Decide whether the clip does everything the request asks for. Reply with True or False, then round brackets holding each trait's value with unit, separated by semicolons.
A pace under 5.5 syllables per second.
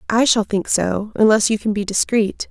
True (4.8 syllables/s)